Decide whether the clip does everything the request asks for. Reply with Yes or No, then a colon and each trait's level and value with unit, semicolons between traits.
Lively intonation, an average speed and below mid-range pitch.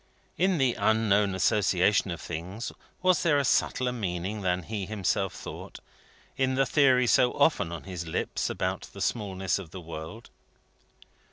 Yes: wide, 5.7 semitones; average, 155 wpm; low, 105 Hz